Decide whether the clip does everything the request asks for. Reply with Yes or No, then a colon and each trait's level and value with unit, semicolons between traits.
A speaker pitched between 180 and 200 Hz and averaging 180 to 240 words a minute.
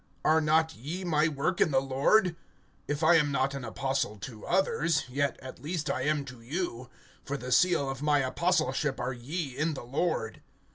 No: medium, 145 Hz; average, 190 wpm